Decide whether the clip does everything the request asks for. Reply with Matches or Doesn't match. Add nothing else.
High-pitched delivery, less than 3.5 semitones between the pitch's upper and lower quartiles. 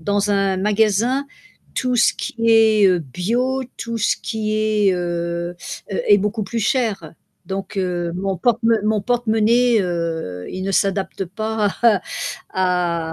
Doesn't match